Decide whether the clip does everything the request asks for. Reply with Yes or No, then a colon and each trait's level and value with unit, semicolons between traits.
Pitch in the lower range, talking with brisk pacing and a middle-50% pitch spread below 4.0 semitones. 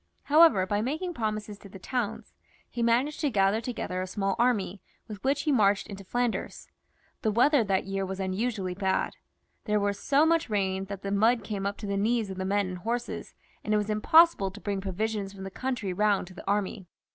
No: high, 205 Hz; fast, 210 wpm; average, 3.4 semitones